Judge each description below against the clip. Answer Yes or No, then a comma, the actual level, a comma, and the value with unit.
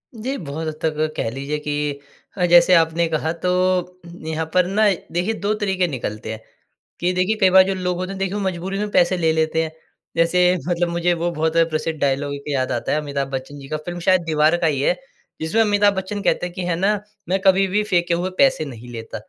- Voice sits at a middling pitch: Yes, medium, 170 Hz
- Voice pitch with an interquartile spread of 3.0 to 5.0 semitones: Yes, average, 3.5 semitones